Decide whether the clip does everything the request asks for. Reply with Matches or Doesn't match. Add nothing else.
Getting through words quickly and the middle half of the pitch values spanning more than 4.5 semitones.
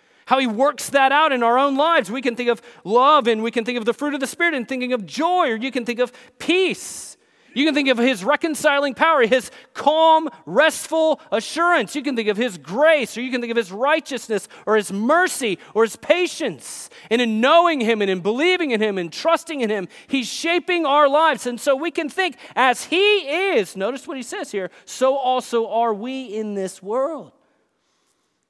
Matches